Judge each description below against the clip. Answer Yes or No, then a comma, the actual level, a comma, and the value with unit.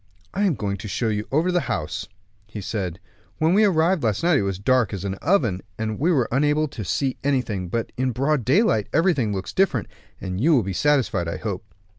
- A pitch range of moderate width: No, wide, 7.3 semitones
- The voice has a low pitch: Yes, low, 120 Hz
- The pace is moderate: No, fast, 220 wpm